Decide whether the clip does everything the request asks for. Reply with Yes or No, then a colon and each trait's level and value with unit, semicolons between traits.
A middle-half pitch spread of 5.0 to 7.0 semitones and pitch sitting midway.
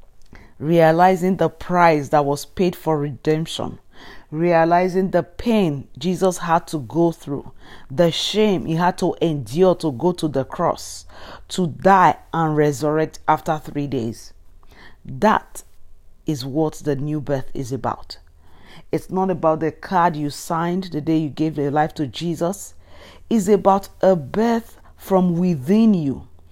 No: average, 4.5 semitones; medium, 160 Hz